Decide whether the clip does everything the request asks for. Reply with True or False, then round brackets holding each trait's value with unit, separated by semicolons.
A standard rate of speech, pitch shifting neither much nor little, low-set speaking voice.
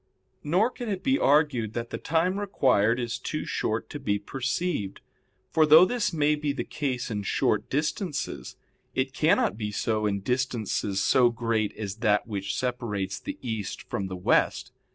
False (170 wpm; 6.3 semitones; 125 Hz)